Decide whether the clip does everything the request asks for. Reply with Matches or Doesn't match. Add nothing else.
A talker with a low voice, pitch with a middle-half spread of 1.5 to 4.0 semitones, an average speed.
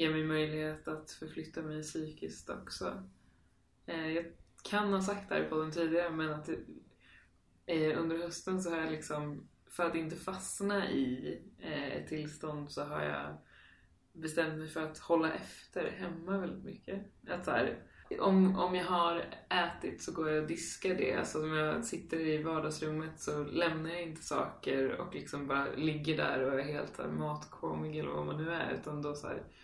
Doesn't match